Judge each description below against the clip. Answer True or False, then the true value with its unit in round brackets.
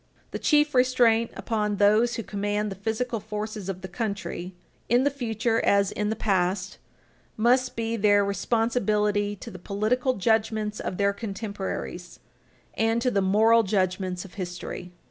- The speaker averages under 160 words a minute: True (150 wpm)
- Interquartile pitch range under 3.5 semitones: True (2.6 semitones)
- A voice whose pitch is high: True (210 Hz)